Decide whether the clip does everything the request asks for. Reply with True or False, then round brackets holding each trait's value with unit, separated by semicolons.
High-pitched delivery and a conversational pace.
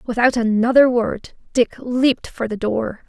True (235 Hz; 155 wpm)